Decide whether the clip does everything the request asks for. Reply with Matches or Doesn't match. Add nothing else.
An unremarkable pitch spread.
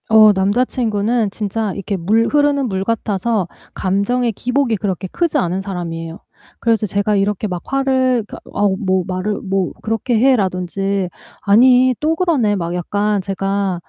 Matches